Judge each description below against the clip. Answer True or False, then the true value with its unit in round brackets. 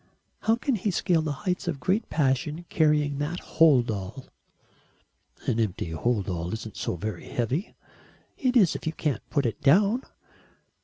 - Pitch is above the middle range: False (145 Hz)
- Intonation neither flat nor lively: False (7.7 semitones)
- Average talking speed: True (165 wpm)